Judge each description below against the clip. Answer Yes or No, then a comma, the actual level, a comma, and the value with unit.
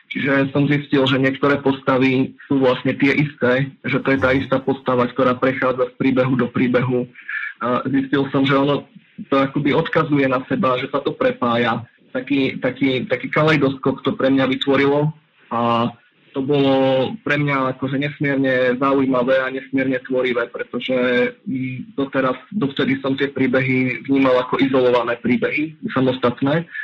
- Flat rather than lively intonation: Yes, narrow, 1.4 semitones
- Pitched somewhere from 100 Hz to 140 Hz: Yes, low, 135 Hz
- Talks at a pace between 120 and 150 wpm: Yes, average, 145 wpm